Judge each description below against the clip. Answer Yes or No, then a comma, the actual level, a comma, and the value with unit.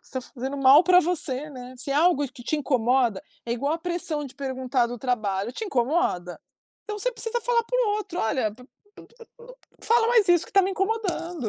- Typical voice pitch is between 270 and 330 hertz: Yes, very high, 290 Hz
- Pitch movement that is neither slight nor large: No, wide, 6.8 semitones